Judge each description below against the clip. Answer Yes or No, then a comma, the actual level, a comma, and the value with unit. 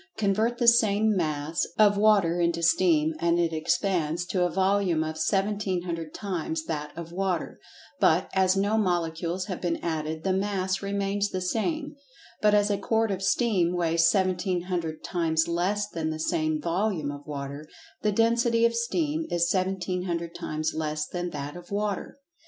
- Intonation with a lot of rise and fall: No, average, 3.7 semitones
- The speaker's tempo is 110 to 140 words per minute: No, average, 155 wpm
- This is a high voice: No, medium, 180 Hz